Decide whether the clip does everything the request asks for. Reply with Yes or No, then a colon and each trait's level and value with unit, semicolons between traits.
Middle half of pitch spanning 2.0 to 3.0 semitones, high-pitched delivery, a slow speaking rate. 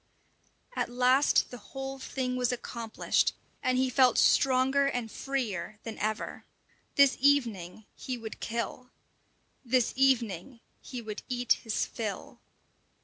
Yes: average, 2.7 semitones; very high, 250 Hz; slow, 125 wpm